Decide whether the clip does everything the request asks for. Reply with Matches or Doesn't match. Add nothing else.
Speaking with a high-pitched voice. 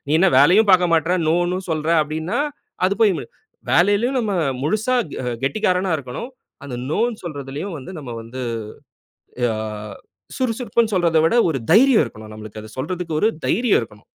Doesn't match